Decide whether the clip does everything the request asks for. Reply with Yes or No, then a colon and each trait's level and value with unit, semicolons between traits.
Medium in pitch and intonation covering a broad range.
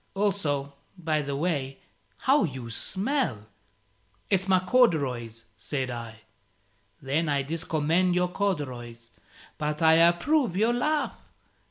Yes: medium, 160 Hz; wide, 5.8 semitones